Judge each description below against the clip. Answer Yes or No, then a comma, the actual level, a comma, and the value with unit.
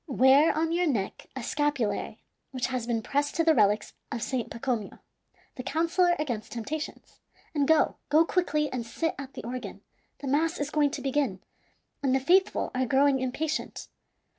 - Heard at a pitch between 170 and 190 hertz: No, very high, 275 Hz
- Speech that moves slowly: No, average, 170 wpm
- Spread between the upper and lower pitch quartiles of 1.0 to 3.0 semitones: No, average, 4.0 semitones